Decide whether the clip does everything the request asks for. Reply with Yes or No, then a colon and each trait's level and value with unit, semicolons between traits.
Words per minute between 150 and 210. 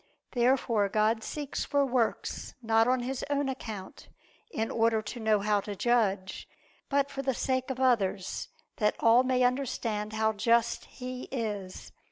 Yes: average, 155 wpm